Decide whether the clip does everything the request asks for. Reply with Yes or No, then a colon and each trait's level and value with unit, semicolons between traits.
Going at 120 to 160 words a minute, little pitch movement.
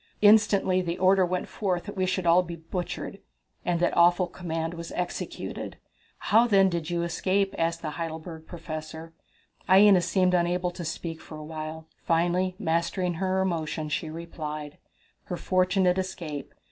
Yes: average, 155 wpm; narrow, 2.2 semitones